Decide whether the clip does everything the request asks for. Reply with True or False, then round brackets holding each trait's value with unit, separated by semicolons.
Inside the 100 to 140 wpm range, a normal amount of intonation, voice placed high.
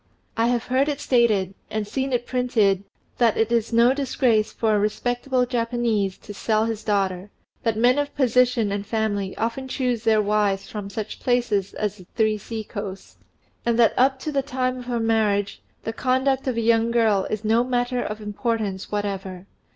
False (190 wpm; 3.0 semitones; 225 Hz)